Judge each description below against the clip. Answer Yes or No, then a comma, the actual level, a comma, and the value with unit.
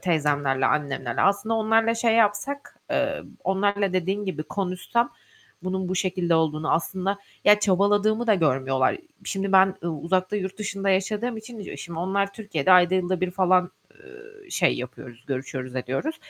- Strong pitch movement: No, average, 3.9 semitones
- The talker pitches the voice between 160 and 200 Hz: Yes, high, 190 Hz